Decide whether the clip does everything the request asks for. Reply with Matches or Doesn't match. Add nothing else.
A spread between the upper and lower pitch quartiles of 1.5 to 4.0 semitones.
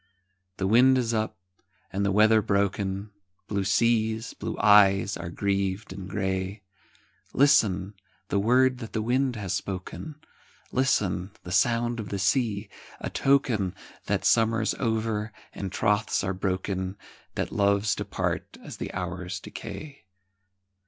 Matches